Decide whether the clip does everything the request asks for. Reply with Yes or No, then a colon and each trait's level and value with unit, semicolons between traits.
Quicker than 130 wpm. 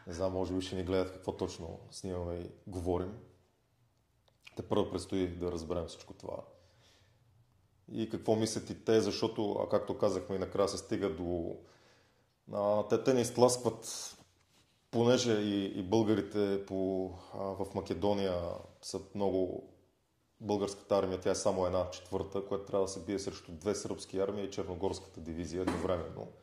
Yes: average, 150 wpm